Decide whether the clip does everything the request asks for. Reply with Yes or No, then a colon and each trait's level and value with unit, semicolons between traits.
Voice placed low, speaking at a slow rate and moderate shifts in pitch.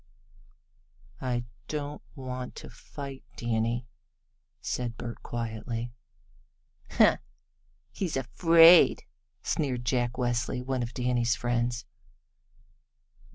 No: low, 125 Hz; slow, 85 wpm; narrow, 1.9 semitones